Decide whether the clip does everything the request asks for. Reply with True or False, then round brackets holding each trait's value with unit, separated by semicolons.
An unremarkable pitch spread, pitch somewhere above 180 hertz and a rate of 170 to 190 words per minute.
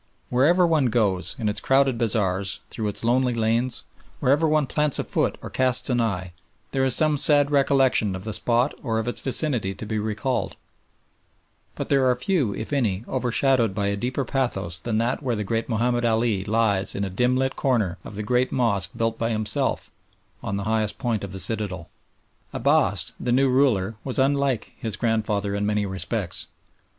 False (4.0 semitones; 115 Hz; 185 wpm)